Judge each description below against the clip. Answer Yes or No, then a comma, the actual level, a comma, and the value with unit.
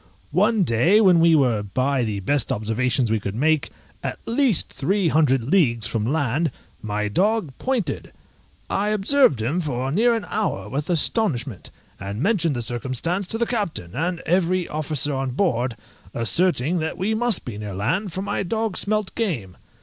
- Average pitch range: No, wide, 8.4 semitones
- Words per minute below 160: No, average, 165 wpm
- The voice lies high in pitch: No, medium, 155 Hz